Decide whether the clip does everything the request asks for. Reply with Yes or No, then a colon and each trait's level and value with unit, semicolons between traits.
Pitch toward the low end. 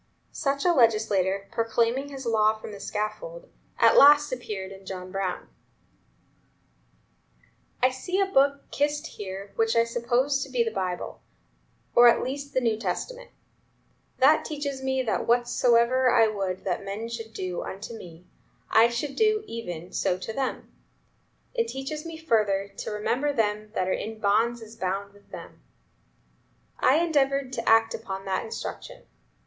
No: high, 230 Hz